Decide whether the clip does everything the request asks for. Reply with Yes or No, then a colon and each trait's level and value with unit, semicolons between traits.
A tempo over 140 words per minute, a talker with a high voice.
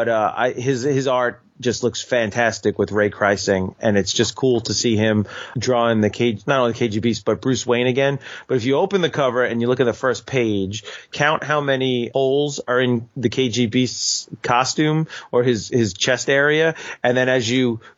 No: fast, 205 wpm; low, 120 Hz